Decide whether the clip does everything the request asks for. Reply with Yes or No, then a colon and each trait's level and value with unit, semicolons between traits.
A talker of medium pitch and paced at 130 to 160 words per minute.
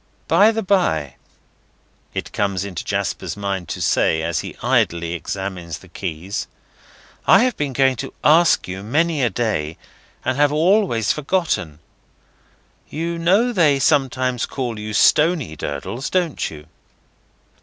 No: low, 125 Hz; slow, 135 wpm